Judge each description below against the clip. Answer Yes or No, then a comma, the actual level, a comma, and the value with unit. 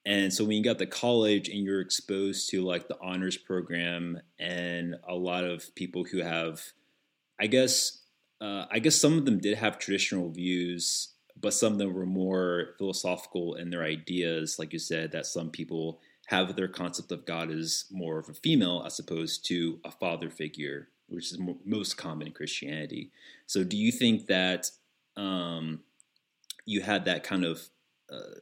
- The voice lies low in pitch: Yes, very low, 90 Hz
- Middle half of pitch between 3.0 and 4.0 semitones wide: No, narrow, 2.6 semitones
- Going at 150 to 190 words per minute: Yes, average, 175 wpm